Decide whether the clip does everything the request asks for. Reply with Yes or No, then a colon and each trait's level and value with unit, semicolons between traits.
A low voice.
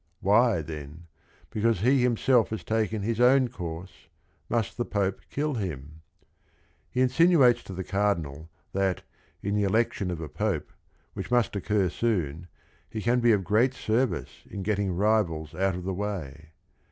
Yes: low, 100 Hz